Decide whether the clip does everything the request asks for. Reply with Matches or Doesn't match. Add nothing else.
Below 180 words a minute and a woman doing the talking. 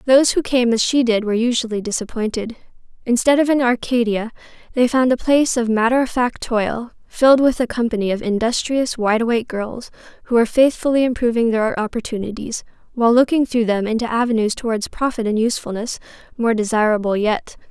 Matches